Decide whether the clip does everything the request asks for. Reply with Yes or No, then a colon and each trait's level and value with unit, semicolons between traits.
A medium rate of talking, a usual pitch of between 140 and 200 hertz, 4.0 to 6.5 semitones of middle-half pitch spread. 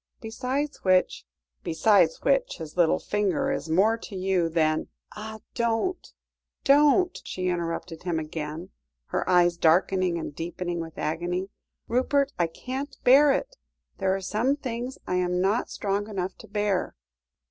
Yes: average, 150 wpm; high, 190 Hz; wide, 5.6 semitones